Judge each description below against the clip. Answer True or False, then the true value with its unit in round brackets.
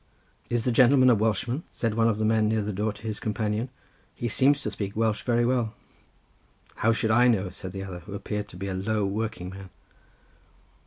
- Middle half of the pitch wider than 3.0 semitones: False (2.5 semitones)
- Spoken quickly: True (210 wpm)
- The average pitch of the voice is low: True (110 Hz)